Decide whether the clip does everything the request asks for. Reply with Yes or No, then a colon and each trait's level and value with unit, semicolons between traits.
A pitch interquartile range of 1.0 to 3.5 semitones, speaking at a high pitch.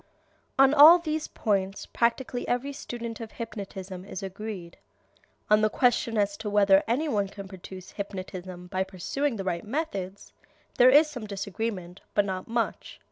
No: average, 4.3 semitones; high, 210 Hz